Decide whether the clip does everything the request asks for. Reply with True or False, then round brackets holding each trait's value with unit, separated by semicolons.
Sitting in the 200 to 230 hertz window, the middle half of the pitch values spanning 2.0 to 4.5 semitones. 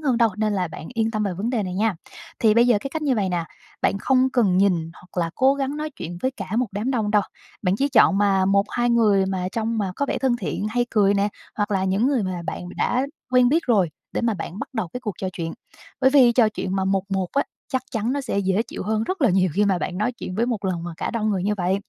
True (210 Hz; 4.2 semitones)